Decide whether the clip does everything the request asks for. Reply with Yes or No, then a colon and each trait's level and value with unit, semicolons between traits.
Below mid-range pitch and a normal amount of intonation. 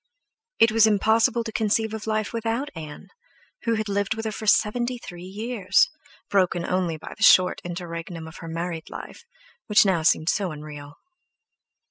No: high, 200 Hz; average, 4.6 semitones